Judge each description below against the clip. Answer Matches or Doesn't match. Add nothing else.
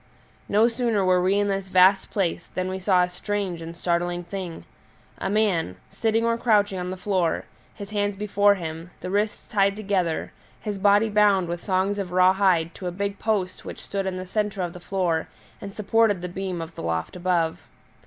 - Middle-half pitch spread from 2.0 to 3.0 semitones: Matches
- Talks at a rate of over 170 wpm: Matches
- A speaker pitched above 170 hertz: Matches